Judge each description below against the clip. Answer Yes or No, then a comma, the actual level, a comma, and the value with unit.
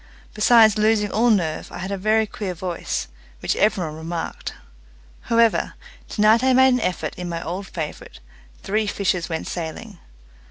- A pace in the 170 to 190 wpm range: No, average, 160 wpm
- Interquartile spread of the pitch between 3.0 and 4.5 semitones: Yes, average, 4.0 semitones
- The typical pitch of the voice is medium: No, high, 200 Hz